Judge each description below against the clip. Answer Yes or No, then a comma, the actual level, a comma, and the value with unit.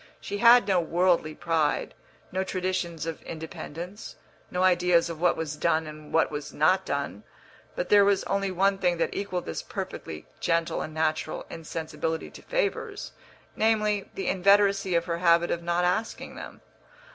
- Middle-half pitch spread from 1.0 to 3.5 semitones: Yes, average, 3.1 semitones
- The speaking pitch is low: No, medium, 175 Hz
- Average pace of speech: Yes, average, 160 wpm